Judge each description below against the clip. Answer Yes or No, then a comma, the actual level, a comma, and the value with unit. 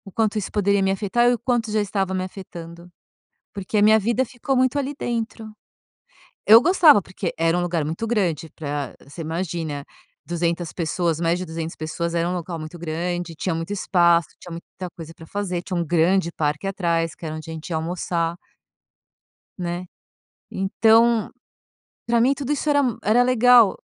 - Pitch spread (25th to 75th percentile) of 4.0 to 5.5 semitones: Yes, average, 4.8 semitones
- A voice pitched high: No, medium, 180 Hz